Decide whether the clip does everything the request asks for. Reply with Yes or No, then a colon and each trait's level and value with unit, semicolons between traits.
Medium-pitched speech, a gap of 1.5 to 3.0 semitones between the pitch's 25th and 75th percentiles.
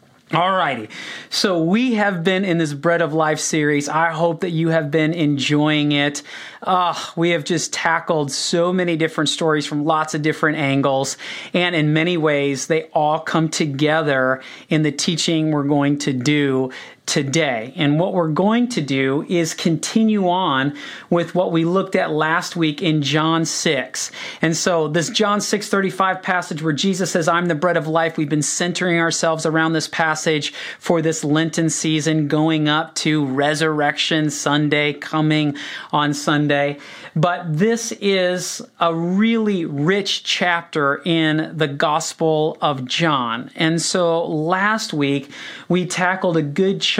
Yes: medium, 160 Hz; average, 2.7 semitones